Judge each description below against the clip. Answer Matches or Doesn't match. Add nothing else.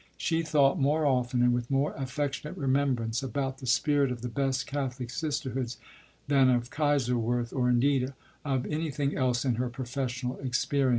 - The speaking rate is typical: Matches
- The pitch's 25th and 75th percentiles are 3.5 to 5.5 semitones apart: Doesn't match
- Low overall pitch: Matches